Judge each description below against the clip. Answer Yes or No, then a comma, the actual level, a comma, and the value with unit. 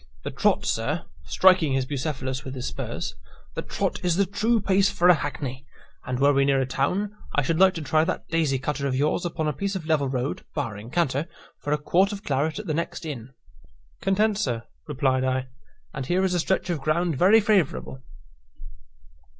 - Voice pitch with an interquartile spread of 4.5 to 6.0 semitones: Yes, wide, 5.4 semitones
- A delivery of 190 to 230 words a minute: Yes, average, 200 wpm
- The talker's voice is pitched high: No, medium, 150 Hz